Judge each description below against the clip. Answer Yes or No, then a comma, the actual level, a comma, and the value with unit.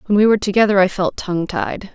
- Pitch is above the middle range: Yes, high, 195 Hz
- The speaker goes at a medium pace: No, fast, 245 wpm